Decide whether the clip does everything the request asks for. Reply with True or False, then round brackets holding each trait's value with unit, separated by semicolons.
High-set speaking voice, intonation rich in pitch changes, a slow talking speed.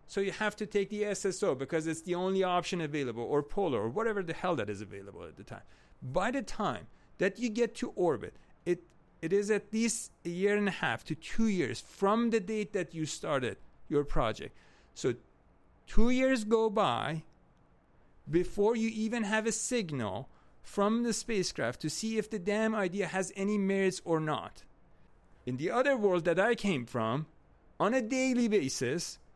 False (195 Hz; 5.8 semitones; 185 wpm)